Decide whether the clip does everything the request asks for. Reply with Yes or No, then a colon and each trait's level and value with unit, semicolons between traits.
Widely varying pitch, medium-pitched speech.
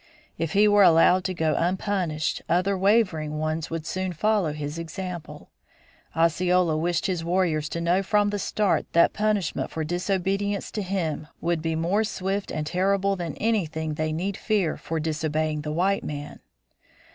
No: average, 3.8 semitones; medium, 175 Hz